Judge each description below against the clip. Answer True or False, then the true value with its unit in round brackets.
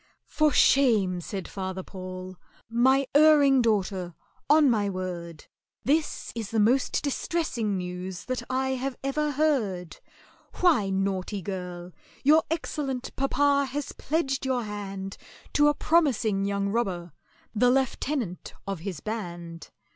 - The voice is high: True (220 Hz)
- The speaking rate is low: True (125 wpm)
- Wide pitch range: True (6.6 semitones)